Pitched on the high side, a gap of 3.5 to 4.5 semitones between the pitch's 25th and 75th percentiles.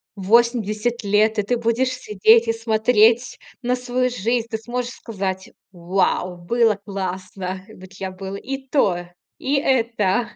Yes: high, 220 Hz; average, 4.0 semitones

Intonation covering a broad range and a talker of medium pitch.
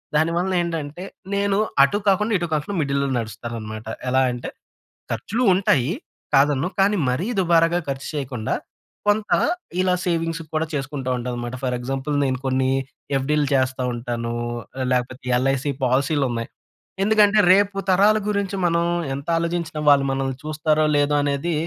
No: average, 5.0 semitones; medium, 145 Hz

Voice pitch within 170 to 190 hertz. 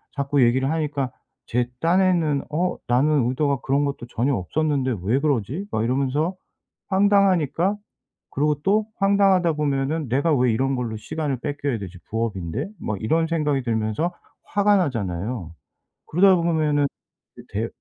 No: medium, 140 Hz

